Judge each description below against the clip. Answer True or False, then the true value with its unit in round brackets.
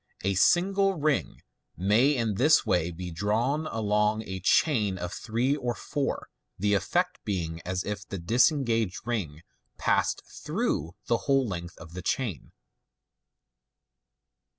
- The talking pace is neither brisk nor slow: False (130 wpm)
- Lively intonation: True (6.5 semitones)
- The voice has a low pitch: True (105 Hz)